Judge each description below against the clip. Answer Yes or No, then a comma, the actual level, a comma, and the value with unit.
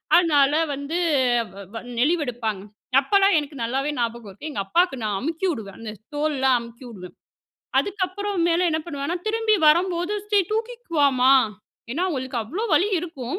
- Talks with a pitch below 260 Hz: No, very high, 295 Hz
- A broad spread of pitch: Yes, wide, 6.4 semitones